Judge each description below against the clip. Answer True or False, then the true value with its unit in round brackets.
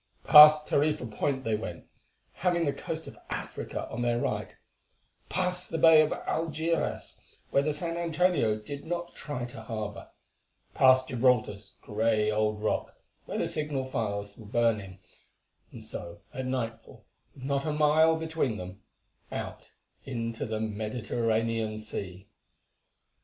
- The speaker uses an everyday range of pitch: False (5.9 semitones)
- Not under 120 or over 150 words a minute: True (135 wpm)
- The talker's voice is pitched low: True (125 Hz)